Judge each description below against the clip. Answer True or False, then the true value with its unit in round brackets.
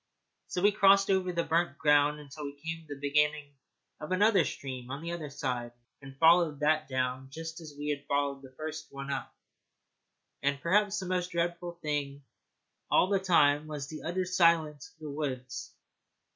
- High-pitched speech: False (150 Hz)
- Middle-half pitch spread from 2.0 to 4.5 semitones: True (3.4 semitones)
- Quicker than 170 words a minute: True (180 wpm)